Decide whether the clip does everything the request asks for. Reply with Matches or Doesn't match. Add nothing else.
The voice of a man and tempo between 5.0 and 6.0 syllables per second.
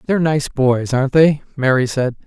Matches